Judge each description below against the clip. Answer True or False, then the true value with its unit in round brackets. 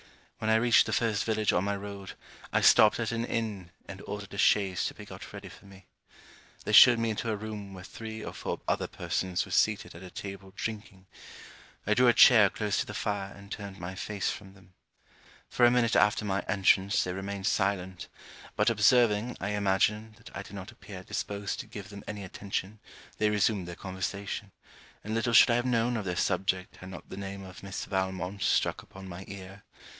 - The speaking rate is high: True (210 wpm)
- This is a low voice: True (100 Hz)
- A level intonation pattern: True (2.1 semitones)